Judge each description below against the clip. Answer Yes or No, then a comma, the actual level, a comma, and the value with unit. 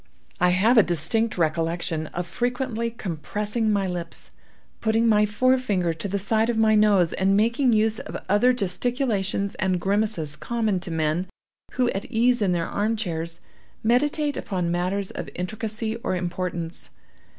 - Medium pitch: No, high, 200 Hz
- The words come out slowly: No, average, 150 wpm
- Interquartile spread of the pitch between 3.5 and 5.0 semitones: Yes, average, 4.2 semitones